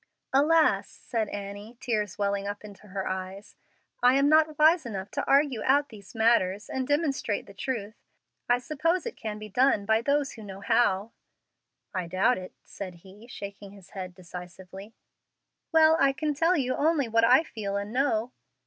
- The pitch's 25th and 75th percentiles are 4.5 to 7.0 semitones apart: Yes, wide, 5.6 semitones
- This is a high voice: Yes, high, 220 Hz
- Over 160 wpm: Yes, average, 175 wpm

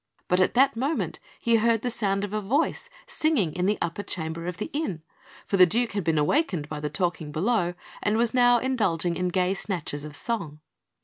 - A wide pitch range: Yes, wide, 5.8 semitones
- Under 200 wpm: No, fast, 205 wpm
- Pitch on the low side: No, high, 195 Hz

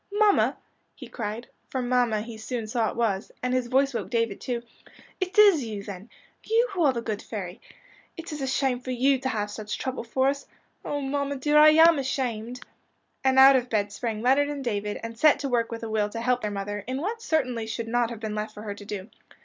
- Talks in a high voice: Yes, high, 245 Hz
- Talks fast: Yes, fast, 230 wpm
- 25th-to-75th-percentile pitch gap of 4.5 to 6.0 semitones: No, average, 3.8 semitones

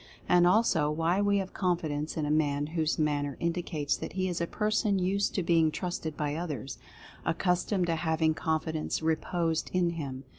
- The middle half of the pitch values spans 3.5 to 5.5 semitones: No, average, 2.7 semitones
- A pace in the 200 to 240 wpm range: No, average, 185 wpm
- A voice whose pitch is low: No, medium, 165 Hz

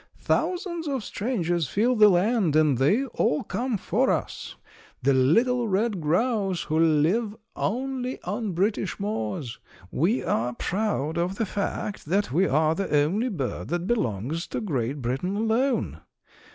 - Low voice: No, high, 195 Hz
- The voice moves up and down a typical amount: No, wide, 6.7 semitones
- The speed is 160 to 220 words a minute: No, average, 145 wpm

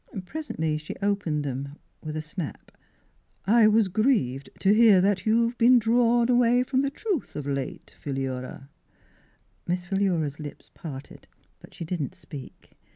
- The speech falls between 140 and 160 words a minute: Yes, average, 155 wpm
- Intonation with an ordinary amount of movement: No, wide, 7.8 semitones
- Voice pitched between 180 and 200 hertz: Yes, medium, 185 Hz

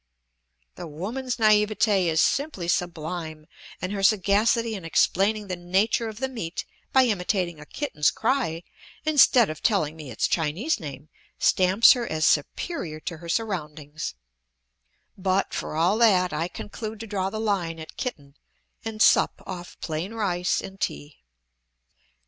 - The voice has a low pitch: No, medium, 185 Hz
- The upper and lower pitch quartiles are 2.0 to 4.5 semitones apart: No, average, 5.3 semitones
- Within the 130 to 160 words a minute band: Yes, average, 145 wpm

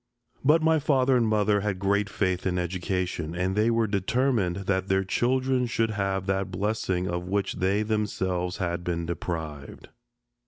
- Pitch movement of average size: Yes, average, 3.3 semitones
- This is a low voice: Yes, very low, 95 Hz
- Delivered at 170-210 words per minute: No, average, 160 wpm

